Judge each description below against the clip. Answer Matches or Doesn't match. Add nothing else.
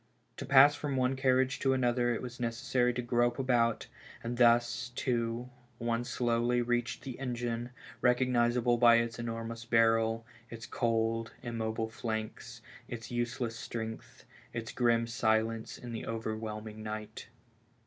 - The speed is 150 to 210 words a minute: Doesn't match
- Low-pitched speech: Matches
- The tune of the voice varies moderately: Doesn't match